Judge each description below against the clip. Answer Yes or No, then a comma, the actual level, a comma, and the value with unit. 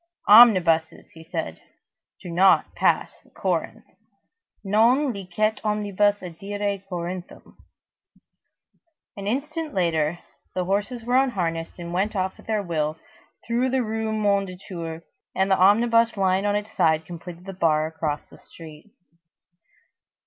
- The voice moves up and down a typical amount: Yes, average, 4.0 semitones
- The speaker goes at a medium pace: No, slow, 125 wpm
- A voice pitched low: No, high, 195 Hz